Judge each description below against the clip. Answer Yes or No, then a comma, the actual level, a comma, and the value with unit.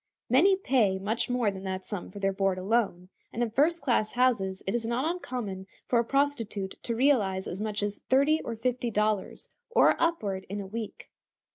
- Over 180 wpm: Yes, average, 190 wpm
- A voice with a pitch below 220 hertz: No, high, 225 Hz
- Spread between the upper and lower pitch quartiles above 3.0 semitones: Yes, average, 4.6 semitones